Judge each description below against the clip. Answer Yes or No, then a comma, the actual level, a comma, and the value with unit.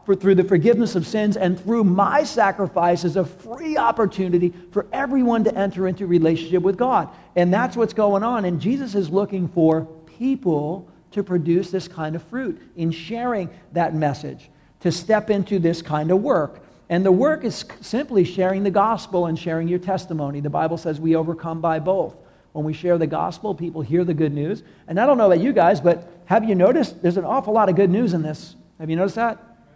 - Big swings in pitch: No, average, 3.6 semitones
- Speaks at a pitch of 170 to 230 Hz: Yes, medium, 185 Hz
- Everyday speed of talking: No, fast, 210 wpm